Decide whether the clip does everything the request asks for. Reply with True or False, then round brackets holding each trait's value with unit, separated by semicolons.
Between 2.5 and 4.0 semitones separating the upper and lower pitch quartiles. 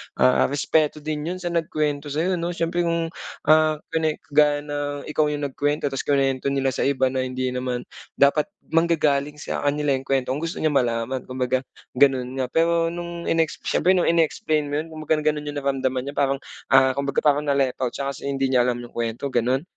True (2.8 semitones)